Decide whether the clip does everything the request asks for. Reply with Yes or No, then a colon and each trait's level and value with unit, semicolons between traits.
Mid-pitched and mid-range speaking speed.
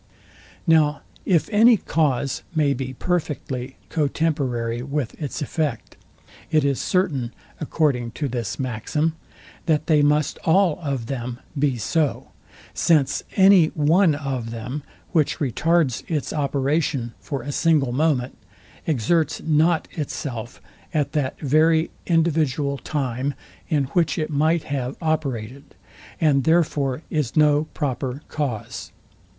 No: medium, 145 Hz; slow, 125 wpm